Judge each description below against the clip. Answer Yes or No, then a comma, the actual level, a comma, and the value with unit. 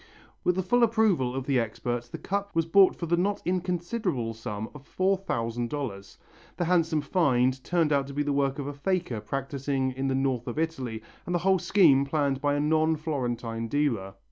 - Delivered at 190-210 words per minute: Yes, average, 200 wpm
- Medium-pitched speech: Yes, medium, 145 Hz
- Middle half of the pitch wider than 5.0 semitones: Yes, wide, 5.4 semitones